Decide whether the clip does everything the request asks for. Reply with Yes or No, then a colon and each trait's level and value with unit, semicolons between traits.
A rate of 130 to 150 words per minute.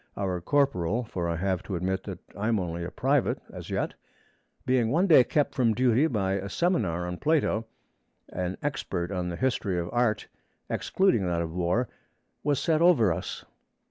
No: average, 175 wpm